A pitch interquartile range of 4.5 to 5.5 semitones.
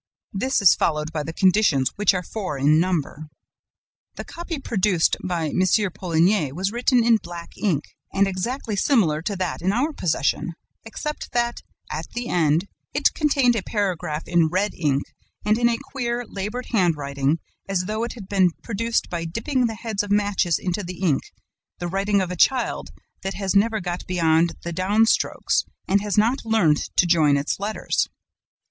Yes: average, 4.8 semitones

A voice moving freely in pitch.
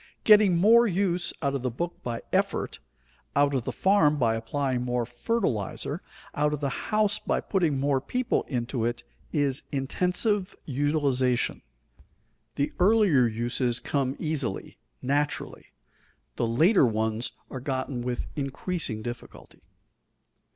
Yes: wide, 6.1 semitones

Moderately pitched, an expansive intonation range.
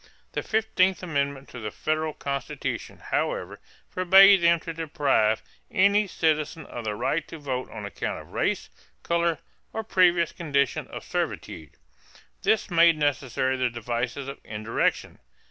No: medium, 150 Hz; average, 5.0 semitones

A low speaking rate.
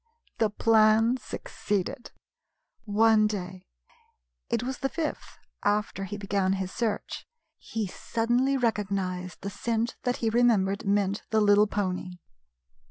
Yes: slow, 120 wpm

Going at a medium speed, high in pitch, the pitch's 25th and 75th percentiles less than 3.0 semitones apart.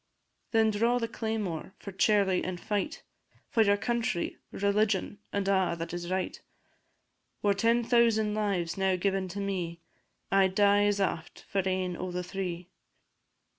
Yes: average, 155 wpm; high, 195 Hz; narrow, 2.6 semitones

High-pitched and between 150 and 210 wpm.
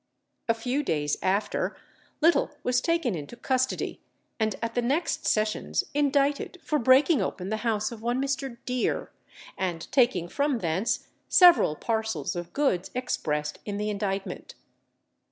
No: high, 235 Hz; average, 140 wpm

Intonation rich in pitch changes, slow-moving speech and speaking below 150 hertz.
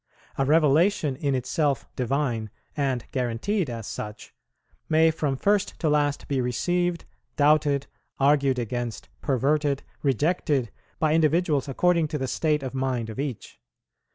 No: average, 3.4 semitones; slow, 130 wpm; medium, 140 Hz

